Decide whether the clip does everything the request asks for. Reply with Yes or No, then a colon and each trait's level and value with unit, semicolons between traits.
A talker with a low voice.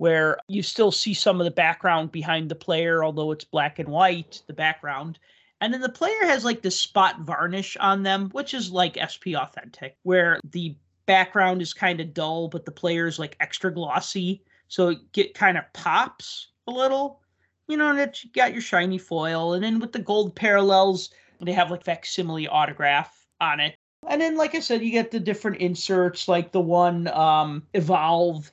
No: medium, 180 Hz